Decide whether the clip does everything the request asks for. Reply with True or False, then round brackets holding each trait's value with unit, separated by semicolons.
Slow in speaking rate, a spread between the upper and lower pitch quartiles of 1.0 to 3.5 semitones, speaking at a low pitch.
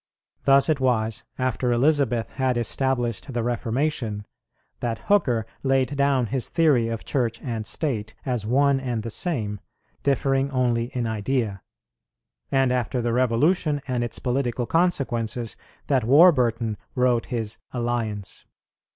True (130 wpm; 2.8 semitones; 125 Hz)